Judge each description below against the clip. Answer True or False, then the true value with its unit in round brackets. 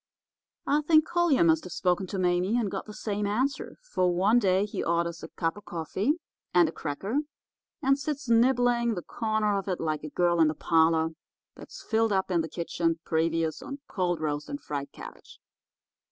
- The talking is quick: False (190 wpm)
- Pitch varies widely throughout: True (6.0 semitones)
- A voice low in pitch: False (185 Hz)